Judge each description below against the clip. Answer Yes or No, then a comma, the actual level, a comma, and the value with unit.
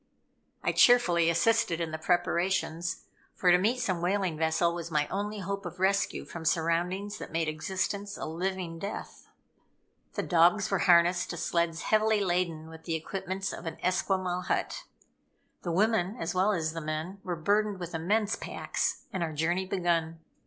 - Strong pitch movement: No, average, 2.9 semitones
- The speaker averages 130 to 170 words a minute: Yes, average, 165 wpm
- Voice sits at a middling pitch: Yes, medium, 175 Hz